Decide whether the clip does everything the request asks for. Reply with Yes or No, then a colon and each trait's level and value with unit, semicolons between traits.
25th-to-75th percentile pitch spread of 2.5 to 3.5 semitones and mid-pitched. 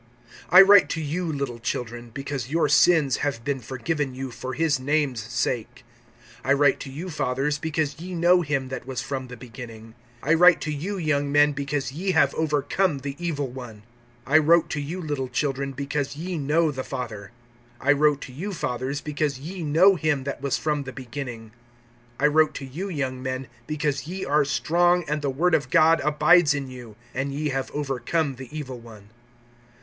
Yes: average, 3.2 semitones; medium, 145 Hz